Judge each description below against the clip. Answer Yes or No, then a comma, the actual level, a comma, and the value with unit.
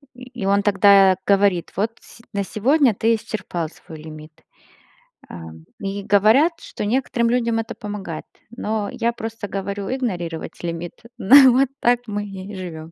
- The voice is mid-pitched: No, high, 205 Hz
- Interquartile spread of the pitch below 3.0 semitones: No, average, 3.6 semitones